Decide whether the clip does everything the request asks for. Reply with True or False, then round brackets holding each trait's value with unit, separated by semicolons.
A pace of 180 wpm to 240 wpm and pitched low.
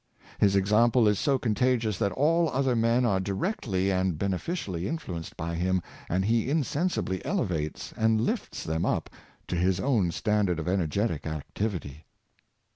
False (150 wpm; 100 Hz)